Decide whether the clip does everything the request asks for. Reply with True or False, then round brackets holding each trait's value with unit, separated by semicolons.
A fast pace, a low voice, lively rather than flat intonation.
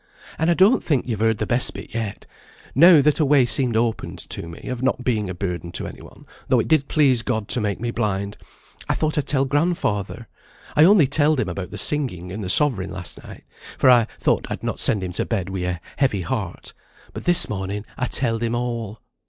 True (225 wpm; 120 Hz; 5.7 semitones)